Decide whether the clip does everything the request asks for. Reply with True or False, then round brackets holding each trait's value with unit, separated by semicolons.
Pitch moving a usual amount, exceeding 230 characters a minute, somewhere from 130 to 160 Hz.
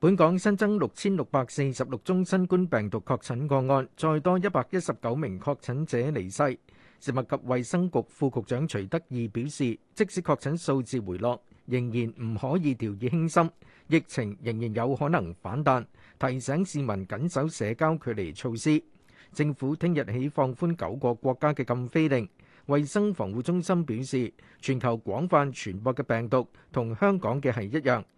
True (4.9 semitones; 265 characters per minute; 135 Hz)